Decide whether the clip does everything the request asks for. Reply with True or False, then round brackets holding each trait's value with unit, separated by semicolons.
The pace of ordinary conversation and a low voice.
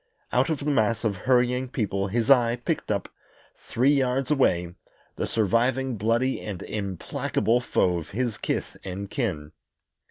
True (150 wpm; 115 Hz)